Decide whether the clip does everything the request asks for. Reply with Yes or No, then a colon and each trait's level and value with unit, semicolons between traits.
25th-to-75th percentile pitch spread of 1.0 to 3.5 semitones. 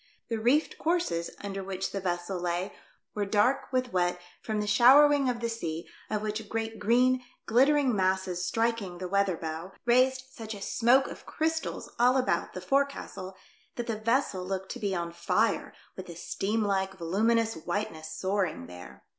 No: average, 4.7 semitones